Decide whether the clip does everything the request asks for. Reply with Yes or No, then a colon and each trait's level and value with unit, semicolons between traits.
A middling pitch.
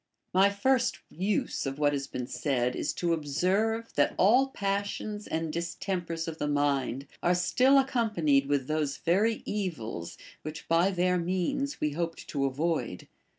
Yes: medium, 170 Hz